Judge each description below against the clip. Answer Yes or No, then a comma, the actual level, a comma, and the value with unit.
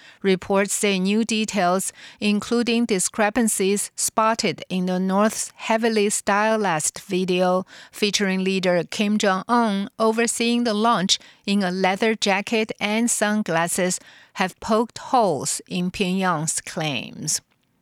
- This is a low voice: No, high, 205 Hz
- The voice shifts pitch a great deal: No, average, 3.1 semitones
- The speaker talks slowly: Yes, slow, 110 wpm